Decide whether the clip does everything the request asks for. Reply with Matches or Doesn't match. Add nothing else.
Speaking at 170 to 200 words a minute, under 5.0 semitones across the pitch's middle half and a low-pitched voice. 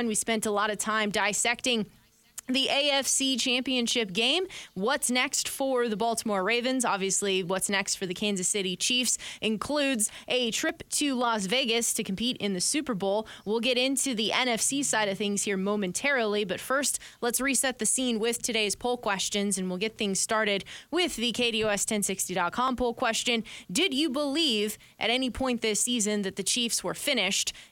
Doesn't match